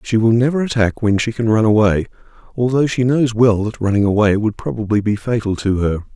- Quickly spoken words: Yes, fast, 215 wpm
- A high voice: No, low, 110 Hz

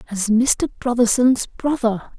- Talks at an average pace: No, slow, 110 wpm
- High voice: Yes, high, 235 Hz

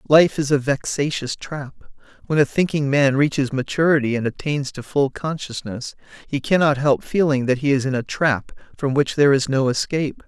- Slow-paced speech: No, average, 185 wpm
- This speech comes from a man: Yes, male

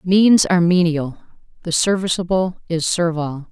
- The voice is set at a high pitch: No, medium, 175 Hz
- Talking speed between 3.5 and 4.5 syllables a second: No, 4.8 syllables/s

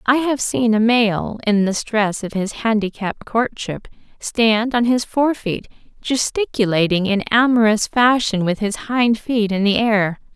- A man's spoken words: No, female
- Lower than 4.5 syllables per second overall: Yes, 4.0 syllables/s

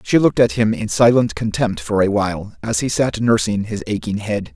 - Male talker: Yes, male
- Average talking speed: No, fast, 225 wpm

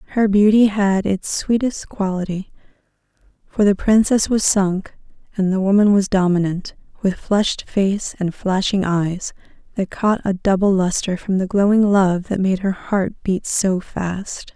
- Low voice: No, high, 195 Hz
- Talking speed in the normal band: Yes, average, 155 wpm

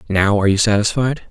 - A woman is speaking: No, male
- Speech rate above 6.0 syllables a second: Yes, 6.7 syllables/s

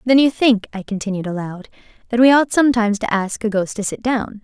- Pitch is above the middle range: Yes, high, 220 Hz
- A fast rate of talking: Yes, fast, 230 wpm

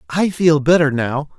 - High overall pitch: No, medium, 155 Hz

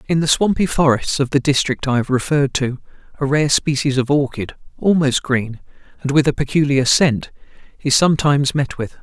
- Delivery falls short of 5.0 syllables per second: No, 5.4 syllables/s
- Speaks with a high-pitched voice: No, medium, 140 Hz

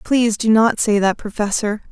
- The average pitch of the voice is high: Yes, high, 215 Hz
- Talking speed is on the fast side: No, average, 190 wpm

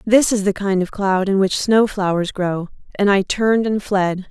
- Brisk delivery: Yes, fast, 225 wpm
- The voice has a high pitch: Yes, high, 200 Hz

